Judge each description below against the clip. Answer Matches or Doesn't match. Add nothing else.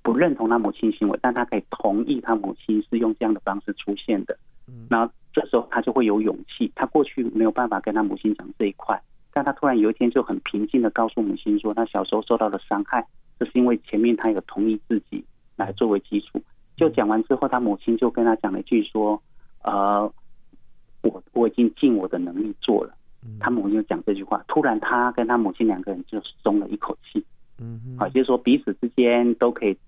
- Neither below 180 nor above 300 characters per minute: Doesn't match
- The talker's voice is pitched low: Matches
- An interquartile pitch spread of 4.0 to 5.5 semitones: Doesn't match